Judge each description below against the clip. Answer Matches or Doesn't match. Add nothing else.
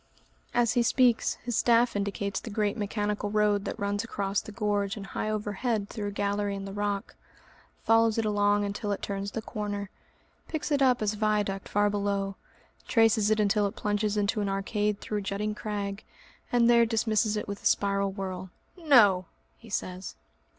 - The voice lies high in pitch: Matches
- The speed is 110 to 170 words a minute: Doesn't match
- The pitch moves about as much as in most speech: Doesn't match